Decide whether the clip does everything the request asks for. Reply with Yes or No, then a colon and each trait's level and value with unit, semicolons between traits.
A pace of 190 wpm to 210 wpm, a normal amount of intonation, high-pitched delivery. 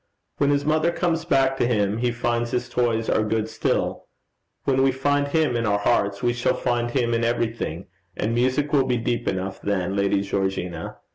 No: average, 200 wpm; average, 4.4 semitones; low, 120 Hz